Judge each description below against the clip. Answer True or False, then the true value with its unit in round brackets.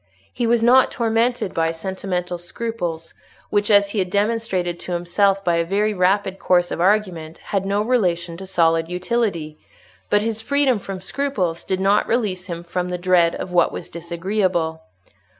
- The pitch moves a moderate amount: True (3.5 semitones)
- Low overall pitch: False (185 Hz)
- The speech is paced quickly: False (170 wpm)